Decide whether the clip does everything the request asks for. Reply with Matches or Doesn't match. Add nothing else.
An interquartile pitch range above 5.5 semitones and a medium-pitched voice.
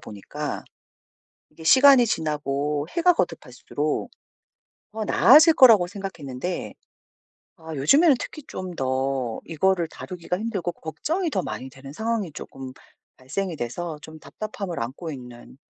Matches